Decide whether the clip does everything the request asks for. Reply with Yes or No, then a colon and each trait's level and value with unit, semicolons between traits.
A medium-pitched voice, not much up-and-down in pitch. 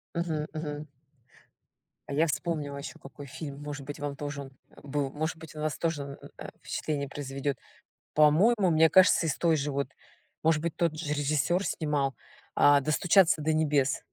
Yes: medium, 150 Hz; narrow, 2.1 semitones